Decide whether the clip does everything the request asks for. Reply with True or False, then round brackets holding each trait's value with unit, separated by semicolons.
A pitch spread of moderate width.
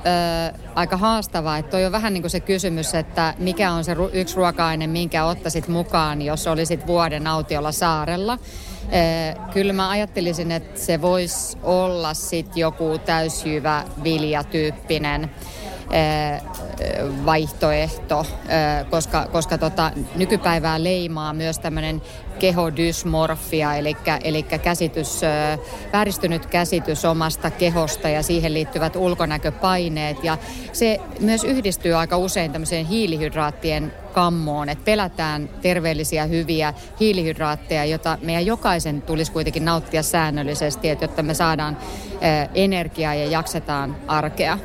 False (2.2 semitones)